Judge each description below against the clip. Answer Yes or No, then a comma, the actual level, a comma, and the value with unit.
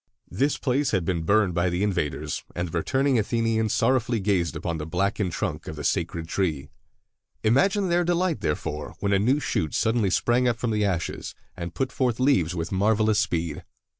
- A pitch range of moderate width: No, wide, 5.9 semitones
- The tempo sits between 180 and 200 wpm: Yes, average, 185 wpm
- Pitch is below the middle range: Yes, low, 105 Hz